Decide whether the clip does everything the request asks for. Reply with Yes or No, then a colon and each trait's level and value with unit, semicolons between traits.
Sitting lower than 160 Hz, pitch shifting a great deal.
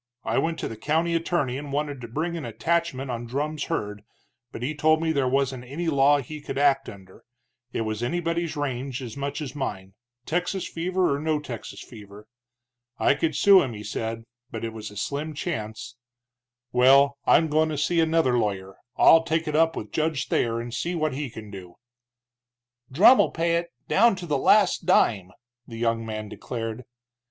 Yes: medium, 140 Hz; wide, 5.8 semitones